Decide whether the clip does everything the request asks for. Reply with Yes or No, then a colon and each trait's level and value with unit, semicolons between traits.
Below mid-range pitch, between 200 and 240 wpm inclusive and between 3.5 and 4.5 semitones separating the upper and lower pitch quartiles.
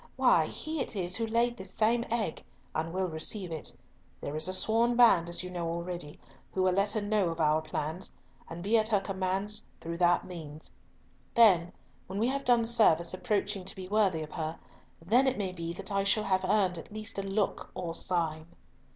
No: high, 190 Hz; fast, 205 wpm; average, 4.2 semitones